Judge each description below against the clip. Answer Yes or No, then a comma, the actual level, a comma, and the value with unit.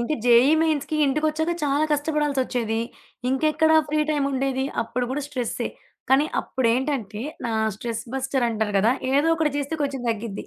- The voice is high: Yes, very high, 270 Hz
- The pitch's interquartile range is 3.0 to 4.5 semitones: Yes, average, 4.0 semitones